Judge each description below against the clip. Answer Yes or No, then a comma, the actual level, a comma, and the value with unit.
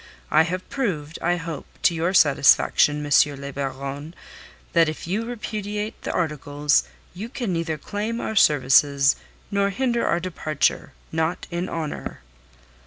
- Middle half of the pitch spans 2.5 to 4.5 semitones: No, average, 5.3 semitones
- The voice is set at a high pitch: No, medium, 165 Hz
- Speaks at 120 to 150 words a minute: Yes, average, 140 wpm